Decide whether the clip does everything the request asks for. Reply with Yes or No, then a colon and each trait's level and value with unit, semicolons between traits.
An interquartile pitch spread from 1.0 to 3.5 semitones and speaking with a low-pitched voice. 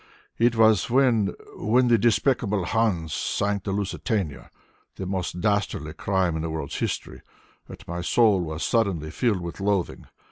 No: average, 4.5 semitones; low, 100 Hz